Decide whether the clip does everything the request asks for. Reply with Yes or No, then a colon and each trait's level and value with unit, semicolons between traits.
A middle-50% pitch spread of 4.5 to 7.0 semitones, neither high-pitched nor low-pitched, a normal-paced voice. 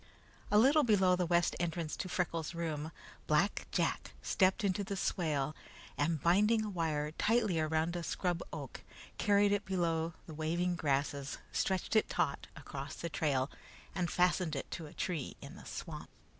No: average, 3.4 semitones; medium, 170 Hz; average, 165 wpm